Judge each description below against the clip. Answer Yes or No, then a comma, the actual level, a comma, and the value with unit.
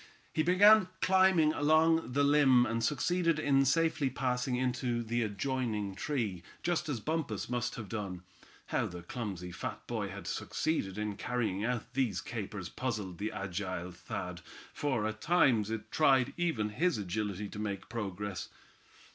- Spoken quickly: No, average, 150 wpm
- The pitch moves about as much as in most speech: No, wide, 6.0 semitones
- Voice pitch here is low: Yes, low, 120 Hz